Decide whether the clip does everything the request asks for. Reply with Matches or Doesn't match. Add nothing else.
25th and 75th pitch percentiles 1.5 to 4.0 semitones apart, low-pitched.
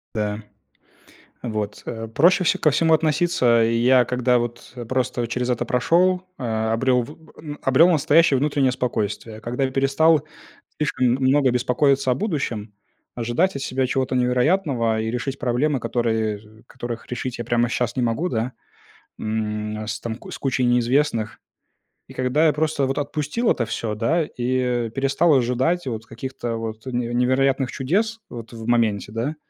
Matches